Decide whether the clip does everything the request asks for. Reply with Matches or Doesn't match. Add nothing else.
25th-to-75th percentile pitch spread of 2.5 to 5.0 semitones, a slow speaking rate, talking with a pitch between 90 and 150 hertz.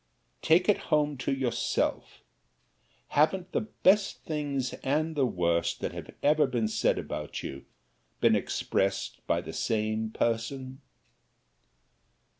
Doesn't match